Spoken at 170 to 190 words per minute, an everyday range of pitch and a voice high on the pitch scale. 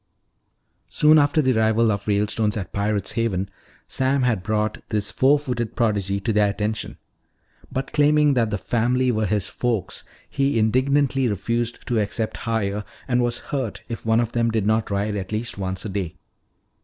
No: average, 175 wpm; average, 3.2 semitones; low, 110 Hz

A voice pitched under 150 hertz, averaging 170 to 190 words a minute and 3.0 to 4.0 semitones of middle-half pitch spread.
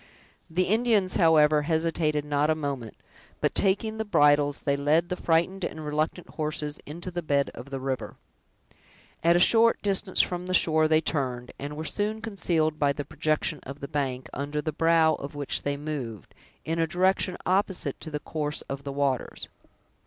No: medium, 155 Hz; average, 180 wpm; average, 3.4 semitones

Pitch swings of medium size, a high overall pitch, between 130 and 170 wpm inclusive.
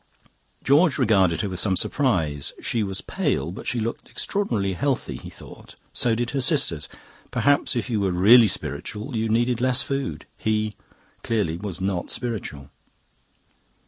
No: average, 4.9 semitones; low, 110 Hz; average, 150 wpm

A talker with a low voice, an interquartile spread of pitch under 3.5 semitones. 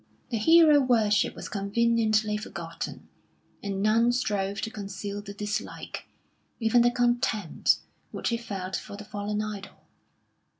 No: high, 215 Hz; narrow, 2.6 semitones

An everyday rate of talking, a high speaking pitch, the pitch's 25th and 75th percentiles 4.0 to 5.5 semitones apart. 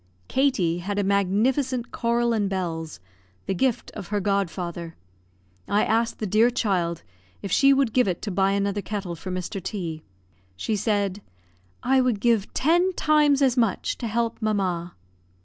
Yes: average, 160 wpm; high, 205 Hz; average, 4.3 semitones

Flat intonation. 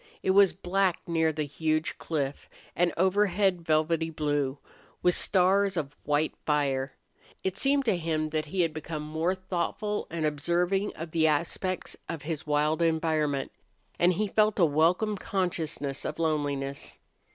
No: average, 3.4 semitones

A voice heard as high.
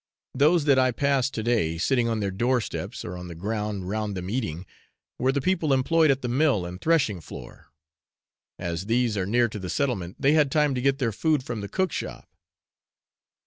No: low, 120 Hz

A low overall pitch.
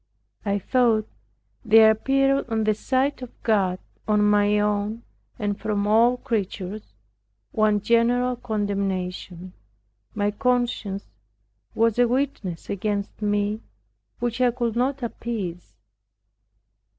No: high, 215 Hz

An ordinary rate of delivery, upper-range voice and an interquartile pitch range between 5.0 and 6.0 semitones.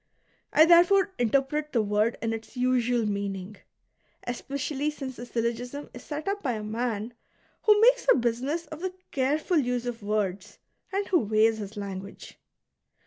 Yes: average, 155 wpm; high, 245 Hz; wide, 5.6 semitones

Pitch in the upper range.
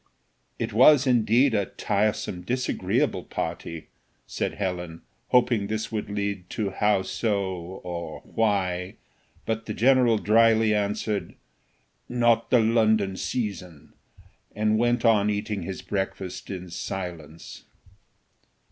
No: low, 105 Hz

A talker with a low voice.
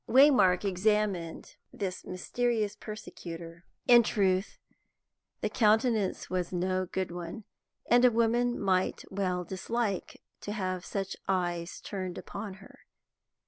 No: high, 195 Hz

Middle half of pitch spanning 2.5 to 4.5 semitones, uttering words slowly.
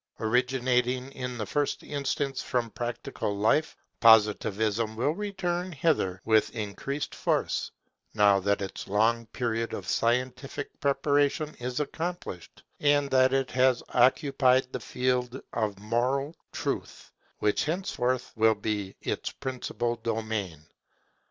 Yes: average, 3.8 semitones; slow, 120 wpm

